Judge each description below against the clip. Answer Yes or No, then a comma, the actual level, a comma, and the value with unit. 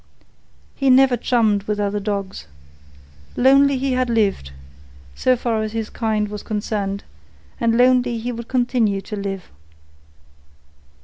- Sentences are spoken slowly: Yes, slow, 130 wpm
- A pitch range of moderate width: Yes, average, 3.3 semitones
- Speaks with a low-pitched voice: No, high, 225 Hz